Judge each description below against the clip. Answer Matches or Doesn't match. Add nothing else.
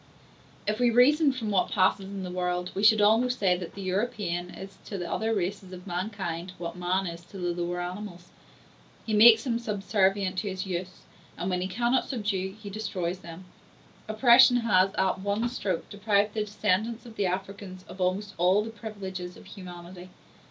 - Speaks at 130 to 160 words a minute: Doesn't match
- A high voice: Matches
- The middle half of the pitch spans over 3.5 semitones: Doesn't match